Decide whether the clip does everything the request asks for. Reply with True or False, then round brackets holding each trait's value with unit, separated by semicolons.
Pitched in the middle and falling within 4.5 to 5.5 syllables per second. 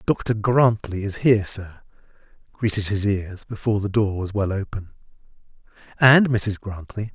False (105 Hz; 4.6 syllables/s)